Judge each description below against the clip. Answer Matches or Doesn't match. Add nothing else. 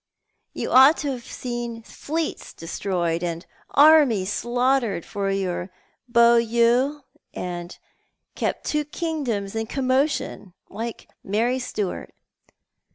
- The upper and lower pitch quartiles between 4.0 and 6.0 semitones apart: Matches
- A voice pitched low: Doesn't match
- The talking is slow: Matches